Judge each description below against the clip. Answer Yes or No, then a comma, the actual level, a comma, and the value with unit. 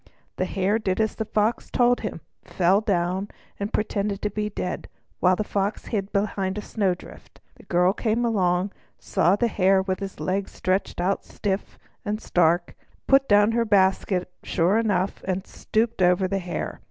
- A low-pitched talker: No, high, 195 Hz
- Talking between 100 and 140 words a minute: No, average, 175 wpm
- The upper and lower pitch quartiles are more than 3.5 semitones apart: No, narrow, 2.4 semitones